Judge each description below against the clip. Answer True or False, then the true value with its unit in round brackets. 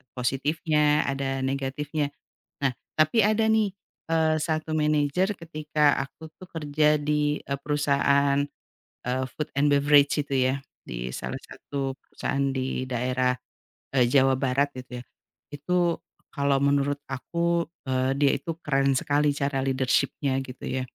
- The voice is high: False (140 Hz)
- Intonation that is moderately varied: False (2.0 semitones)